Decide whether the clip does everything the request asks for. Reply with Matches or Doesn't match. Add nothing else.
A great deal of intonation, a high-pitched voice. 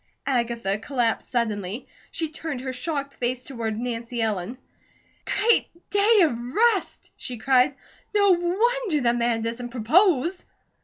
Matches